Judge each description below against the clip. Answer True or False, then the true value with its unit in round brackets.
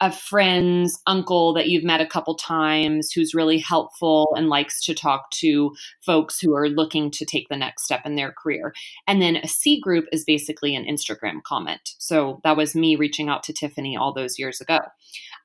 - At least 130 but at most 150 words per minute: False (200 wpm)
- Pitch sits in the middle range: True (155 Hz)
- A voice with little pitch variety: True (1.7 semitones)